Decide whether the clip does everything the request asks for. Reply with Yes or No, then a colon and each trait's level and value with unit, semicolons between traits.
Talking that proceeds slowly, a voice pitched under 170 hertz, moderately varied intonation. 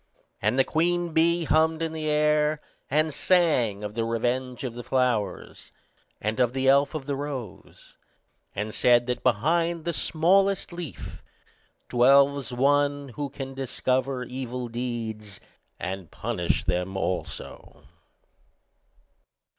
Yes: slow, 125 wpm; low, 135 Hz; average, 4.5 semitones